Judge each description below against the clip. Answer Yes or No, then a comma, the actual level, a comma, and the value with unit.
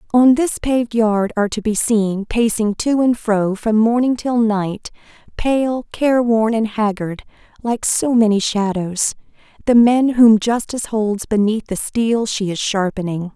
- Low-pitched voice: No, high, 220 Hz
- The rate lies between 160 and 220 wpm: No, average, 150 wpm